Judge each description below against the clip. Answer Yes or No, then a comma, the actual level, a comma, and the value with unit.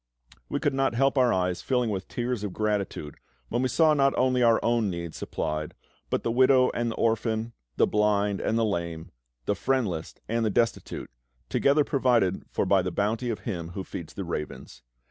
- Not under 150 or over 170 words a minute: No, average, 190 wpm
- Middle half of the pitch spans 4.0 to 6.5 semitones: Yes, average, 4.9 semitones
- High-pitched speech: No, low, 115 Hz